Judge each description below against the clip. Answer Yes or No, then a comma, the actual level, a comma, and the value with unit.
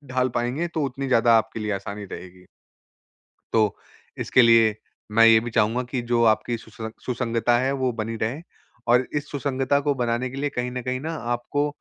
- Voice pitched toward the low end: Yes, low, 120 Hz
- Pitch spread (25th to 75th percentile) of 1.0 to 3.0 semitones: Yes, narrow, 2.5 semitones